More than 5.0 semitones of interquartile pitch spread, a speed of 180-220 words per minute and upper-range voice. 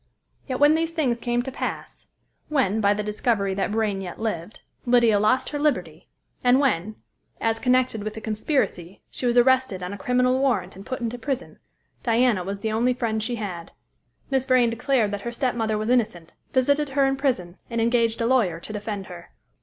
No: average, 3.8 semitones; average, 195 wpm; high, 230 Hz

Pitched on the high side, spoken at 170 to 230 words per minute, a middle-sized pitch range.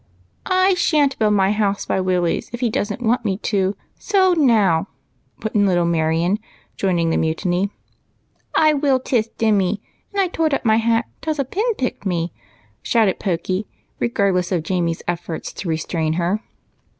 No: high, 205 Hz; average, 175 wpm; wide, 5.8 semitones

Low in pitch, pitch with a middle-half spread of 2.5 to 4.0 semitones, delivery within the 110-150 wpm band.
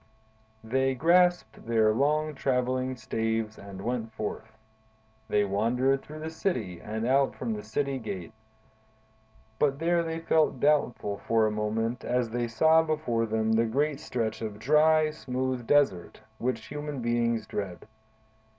No: low, 120 Hz; average, 4.7 semitones; average, 140 wpm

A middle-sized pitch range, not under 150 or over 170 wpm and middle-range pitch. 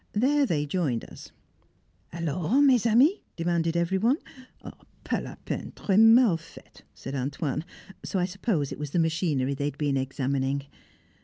No: wide, 6.8 semitones; average, 155 wpm; medium, 165 Hz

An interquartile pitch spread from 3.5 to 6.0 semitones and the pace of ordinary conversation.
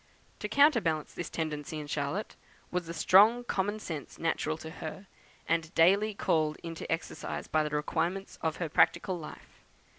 Yes: average, 3.9 semitones; average, 155 wpm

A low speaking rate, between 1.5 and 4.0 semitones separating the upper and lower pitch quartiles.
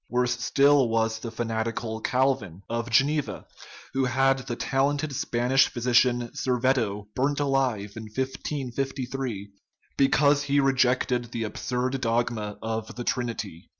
Yes: slow, 130 wpm; average, 2.9 semitones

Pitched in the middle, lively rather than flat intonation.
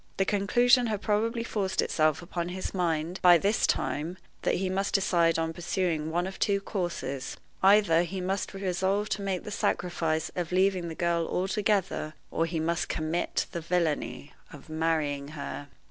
No: medium, 180 Hz; average, 3.1 semitones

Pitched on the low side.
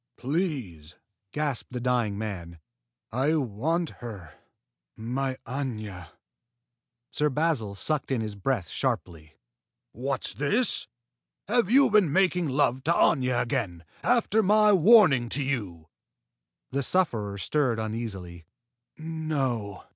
Yes: low, 130 Hz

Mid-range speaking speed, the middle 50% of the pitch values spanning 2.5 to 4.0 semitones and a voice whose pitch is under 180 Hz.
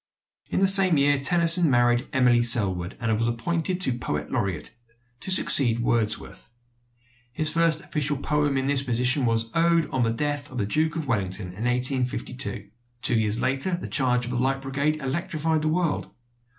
No: average, 175 wpm; average, 4.7 semitones; low, 135 Hz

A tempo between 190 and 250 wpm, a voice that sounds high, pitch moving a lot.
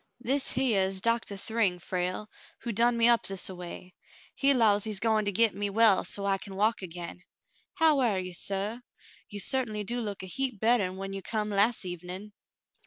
No: average, 200 wpm; high, 205 Hz; average, 3.4 semitones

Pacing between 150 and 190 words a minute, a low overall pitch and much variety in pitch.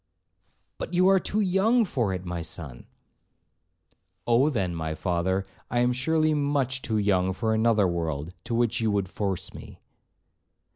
Yes: average, 155 wpm; low, 110 Hz; wide, 6.7 semitones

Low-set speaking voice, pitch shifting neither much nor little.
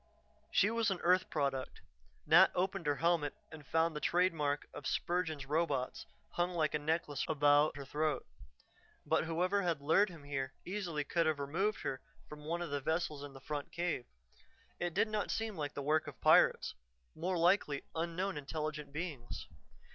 No: medium, 160 Hz; average, 3.3 semitones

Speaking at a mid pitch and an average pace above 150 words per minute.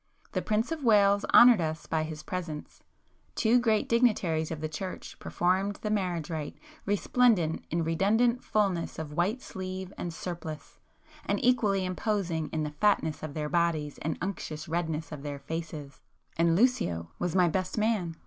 Yes: medium, 175 Hz; average, 160 wpm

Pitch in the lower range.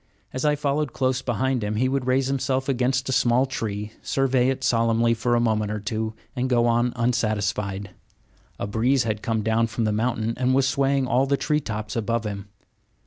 Yes: low, 120 Hz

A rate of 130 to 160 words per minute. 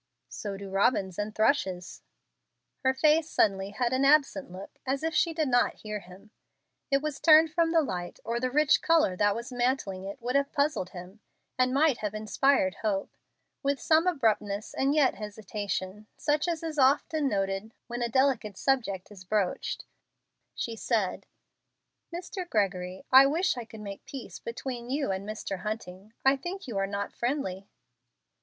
No: average, 170 wpm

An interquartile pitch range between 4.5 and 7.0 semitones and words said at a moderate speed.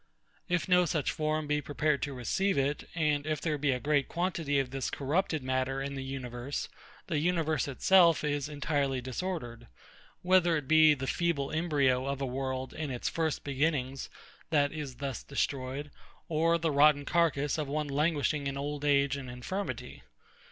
No: narrow, 2.6 semitones; average, 170 wpm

